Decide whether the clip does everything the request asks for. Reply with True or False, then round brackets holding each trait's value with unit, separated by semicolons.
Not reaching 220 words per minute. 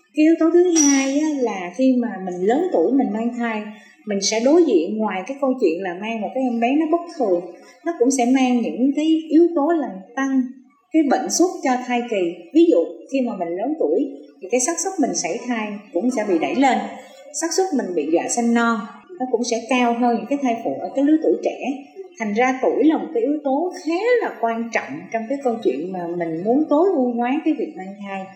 False (240 wpm)